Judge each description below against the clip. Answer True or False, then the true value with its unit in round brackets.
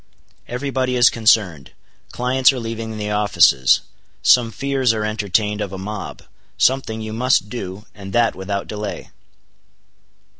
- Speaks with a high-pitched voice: False (110 Hz)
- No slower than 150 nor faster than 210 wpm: False (140 wpm)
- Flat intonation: False (3.3 semitones)